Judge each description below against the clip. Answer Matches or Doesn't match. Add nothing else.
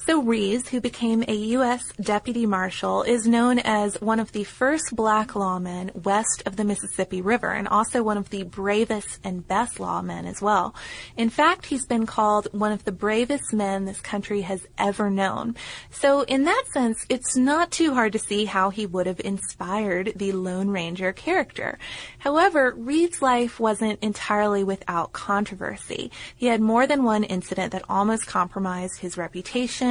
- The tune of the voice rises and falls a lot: Doesn't match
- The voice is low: Doesn't match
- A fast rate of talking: Doesn't match